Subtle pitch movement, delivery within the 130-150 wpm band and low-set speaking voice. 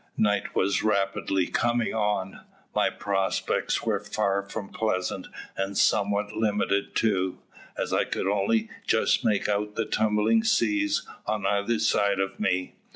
Yes: narrow, 1.9 semitones; average, 140 wpm; low, 105 Hz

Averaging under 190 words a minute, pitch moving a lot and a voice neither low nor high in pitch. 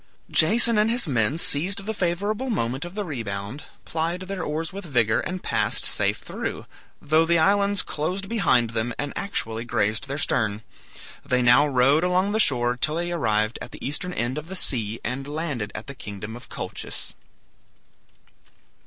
Yes: average, 170 wpm; wide, 7.2 semitones; medium, 150 Hz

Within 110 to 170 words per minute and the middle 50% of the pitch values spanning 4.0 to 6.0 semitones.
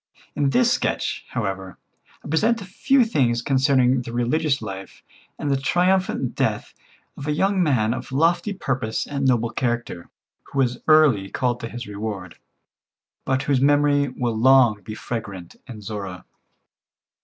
Yes: average, 150 wpm; average, 4.7 semitones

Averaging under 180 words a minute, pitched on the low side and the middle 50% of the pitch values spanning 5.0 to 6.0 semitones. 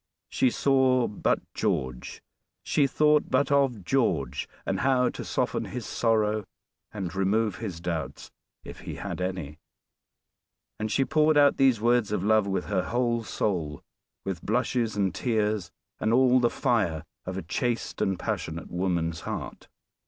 Yes: average, 150 wpm; low, 110 Hz; average, 5.3 semitones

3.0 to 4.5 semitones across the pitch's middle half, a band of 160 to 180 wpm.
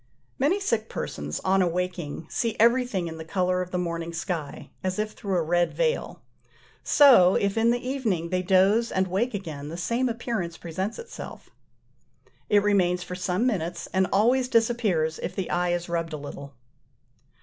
No: average, 5.0 semitones; average, 170 wpm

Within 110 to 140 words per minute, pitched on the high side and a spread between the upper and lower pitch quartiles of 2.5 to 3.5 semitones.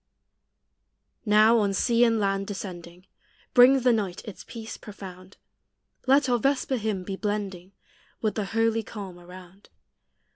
Yes: slow, 135 wpm; high, 210 Hz; average, 3.1 semitones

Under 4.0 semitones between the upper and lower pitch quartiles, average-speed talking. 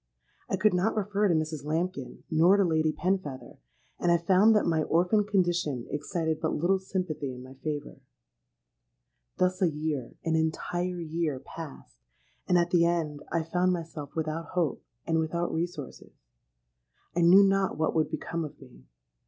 Yes: average, 2.7 semitones; average, 155 wpm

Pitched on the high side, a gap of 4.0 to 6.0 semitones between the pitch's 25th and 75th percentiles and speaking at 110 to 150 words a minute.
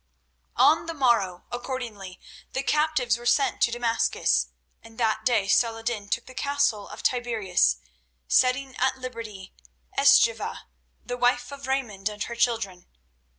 No: high, 235 Hz; average, 3.6 semitones; slow, 135 wpm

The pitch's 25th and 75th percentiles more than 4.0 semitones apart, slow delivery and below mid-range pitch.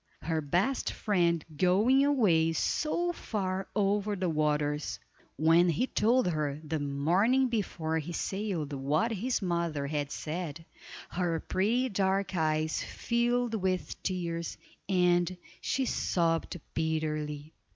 No: average, 4.7 semitones; slow, 120 wpm; medium, 175 Hz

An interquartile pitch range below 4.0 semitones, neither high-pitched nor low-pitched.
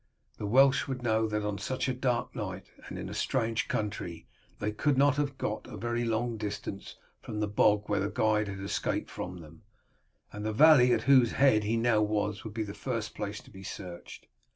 No: average, 3.1 semitones; low, 110 Hz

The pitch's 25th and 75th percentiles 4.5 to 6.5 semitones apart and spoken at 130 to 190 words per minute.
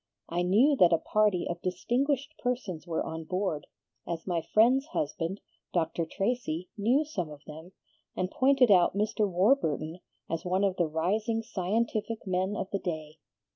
Yes: average, 5.1 semitones; average, 160 wpm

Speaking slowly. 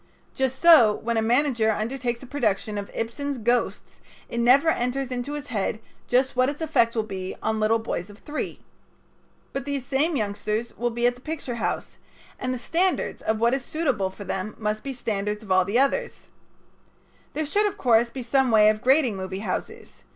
No: average, 195 wpm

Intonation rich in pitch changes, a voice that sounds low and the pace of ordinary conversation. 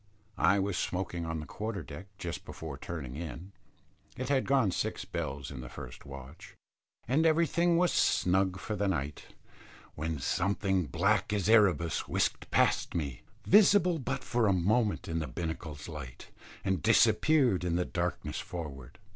Yes: wide, 6.3 semitones; very low, 90 Hz; average, 155 wpm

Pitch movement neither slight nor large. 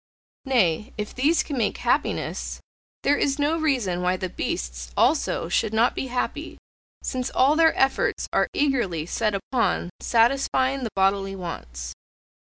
No: wide, 6.7 semitones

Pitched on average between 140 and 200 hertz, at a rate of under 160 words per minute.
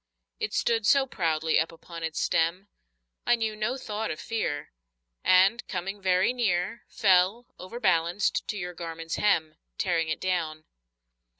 Yes: medium, 185 Hz; average, 140 wpm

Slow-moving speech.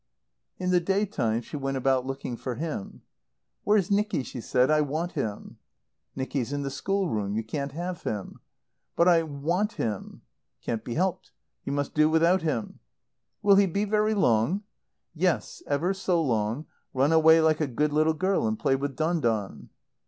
No: average, 175 wpm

